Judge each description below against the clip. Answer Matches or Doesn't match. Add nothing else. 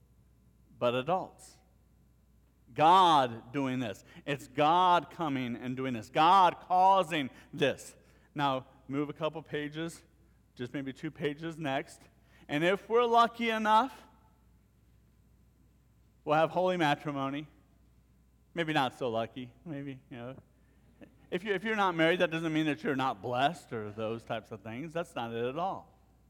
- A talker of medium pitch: Matches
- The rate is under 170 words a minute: Matches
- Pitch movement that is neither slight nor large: Doesn't match